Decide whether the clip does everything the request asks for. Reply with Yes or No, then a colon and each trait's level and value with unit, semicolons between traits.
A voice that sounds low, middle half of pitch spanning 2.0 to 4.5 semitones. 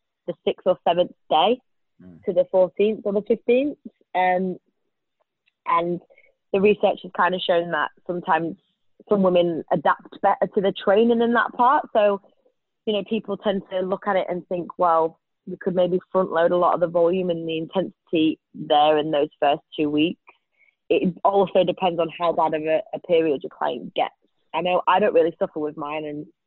No: medium, 180 Hz; average, 3.4 semitones